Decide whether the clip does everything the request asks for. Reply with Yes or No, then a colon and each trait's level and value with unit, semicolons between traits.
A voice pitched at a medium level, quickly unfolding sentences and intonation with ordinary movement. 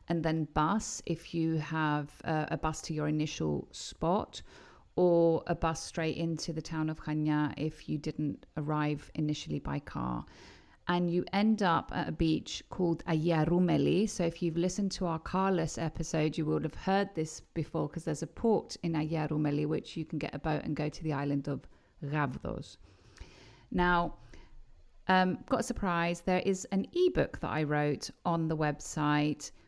No: medium, 160 Hz; fast, 175 wpm; narrow, 2.3 semitones